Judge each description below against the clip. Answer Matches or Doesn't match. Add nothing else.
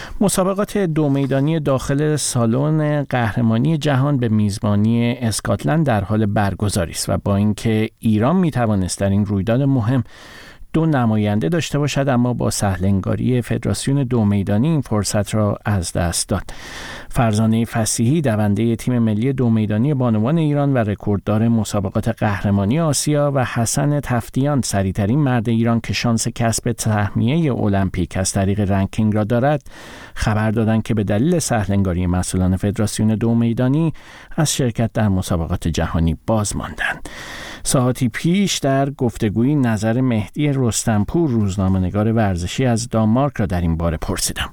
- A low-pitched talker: Matches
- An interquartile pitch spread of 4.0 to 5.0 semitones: Matches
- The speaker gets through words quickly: Doesn't match